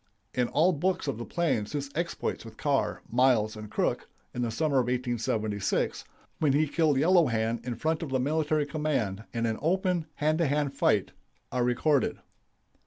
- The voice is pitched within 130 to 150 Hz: Yes, low, 135 Hz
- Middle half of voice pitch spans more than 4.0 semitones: Yes, average, 4.9 semitones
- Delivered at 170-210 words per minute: Yes, average, 175 wpm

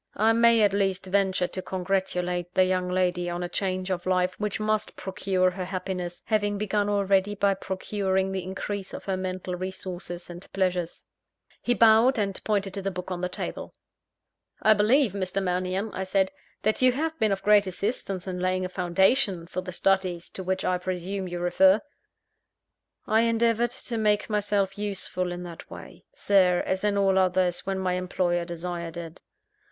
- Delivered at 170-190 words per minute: Yes, average, 180 wpm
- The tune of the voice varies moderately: No, narrow, 2.1 semitones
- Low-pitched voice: No, high, 190 Hz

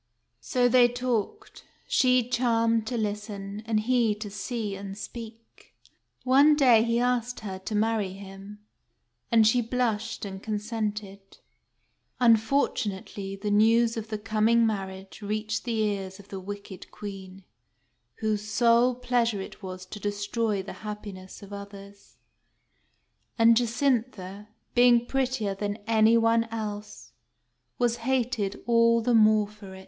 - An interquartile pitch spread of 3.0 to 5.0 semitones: No, narrow, 2.5 semitones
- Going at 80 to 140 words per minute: Yes, slow, 135 wpm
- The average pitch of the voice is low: No, high, 220 Hz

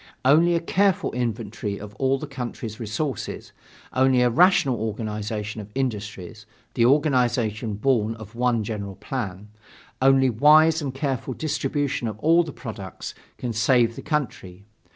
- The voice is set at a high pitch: No, low, 120 Hz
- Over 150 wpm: No, average, 140 wpm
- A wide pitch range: No, average, 4.3 semitones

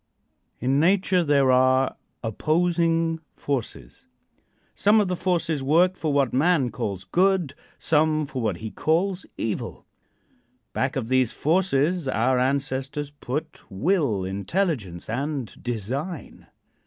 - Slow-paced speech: Yes, slow, 115 wpm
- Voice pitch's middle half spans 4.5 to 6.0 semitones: Yes, average, 4.9 semitones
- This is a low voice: No, medium, 145 Hz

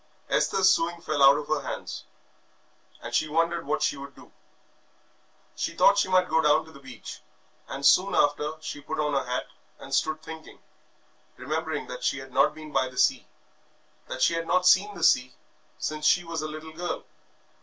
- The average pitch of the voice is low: No, medium, 155 Hz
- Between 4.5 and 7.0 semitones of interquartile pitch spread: No, average, 3.1 semitones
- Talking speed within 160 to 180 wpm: No, average, 195 wpm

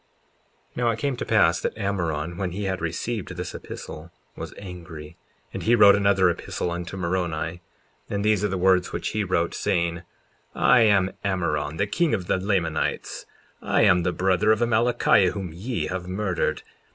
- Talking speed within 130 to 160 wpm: No, average, 180 wpm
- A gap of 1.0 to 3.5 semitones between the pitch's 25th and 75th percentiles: Yes, average, 3.1 semitones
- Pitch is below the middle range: Yes, very low, 95 Hz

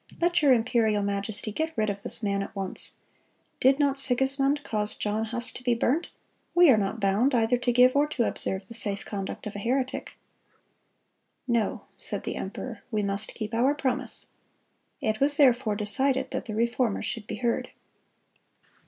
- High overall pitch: Yes, high, 235 Hz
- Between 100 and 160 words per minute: No, average, 175 wpm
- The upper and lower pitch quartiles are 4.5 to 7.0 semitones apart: No, average, 4.1 semitones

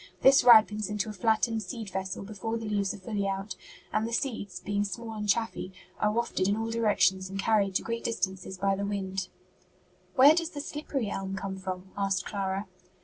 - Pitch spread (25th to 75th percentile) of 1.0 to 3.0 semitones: Yes, average, 2.7 semitones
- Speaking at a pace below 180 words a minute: No, average, 190 wpm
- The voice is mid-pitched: No, high, 205 Hz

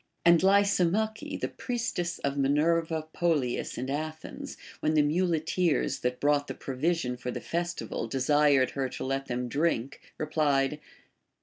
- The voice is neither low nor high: Yes, medium, 150 Hz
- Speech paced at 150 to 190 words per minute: No, average, 140 wpm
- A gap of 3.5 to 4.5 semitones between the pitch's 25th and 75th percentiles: Yes, average, 4.0 semitones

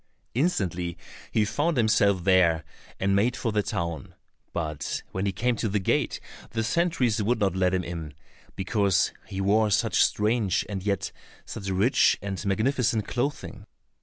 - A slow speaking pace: No, average, 155 wpm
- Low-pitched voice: Yes, low, 100 Hz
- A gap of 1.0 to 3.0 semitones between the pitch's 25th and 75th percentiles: No, average, 3.4 semitones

